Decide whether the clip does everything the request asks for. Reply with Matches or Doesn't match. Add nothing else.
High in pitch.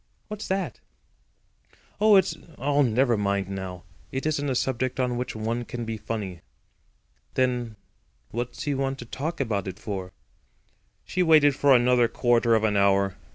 Doesn't match